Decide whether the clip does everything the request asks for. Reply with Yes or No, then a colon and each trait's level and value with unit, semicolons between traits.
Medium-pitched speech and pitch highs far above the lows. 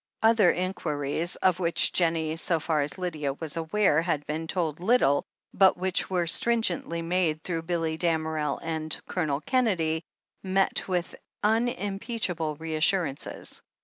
No: medium, 170 Hz; average, 2.9 semitones